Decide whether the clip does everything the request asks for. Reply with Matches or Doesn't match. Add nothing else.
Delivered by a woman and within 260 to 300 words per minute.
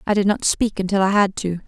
Matches